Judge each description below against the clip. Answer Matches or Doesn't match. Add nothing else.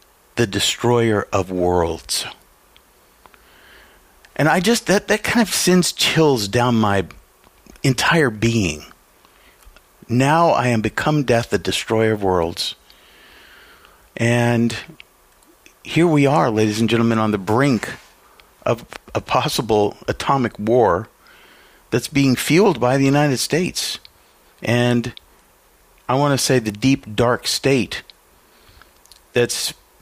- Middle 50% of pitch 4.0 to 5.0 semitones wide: Matches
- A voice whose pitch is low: Matches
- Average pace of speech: Doesn't match